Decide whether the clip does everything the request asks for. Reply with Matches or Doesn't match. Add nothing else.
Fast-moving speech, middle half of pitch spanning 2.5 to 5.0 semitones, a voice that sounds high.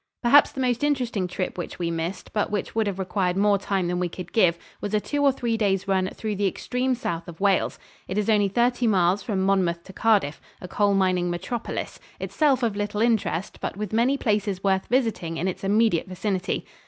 Matches